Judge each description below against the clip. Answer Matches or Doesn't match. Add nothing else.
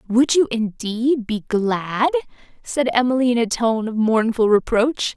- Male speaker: Doesn't match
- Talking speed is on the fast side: Doesn't match